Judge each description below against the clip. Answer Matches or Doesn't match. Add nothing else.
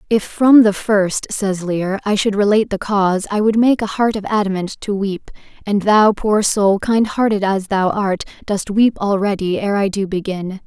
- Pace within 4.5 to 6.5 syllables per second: Matches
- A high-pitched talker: Matches